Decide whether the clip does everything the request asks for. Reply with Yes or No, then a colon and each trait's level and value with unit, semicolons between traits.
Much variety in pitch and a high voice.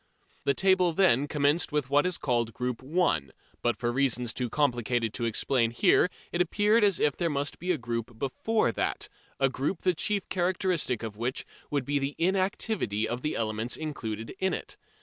No: wide, 6.9 semitones; medium, 140 Hz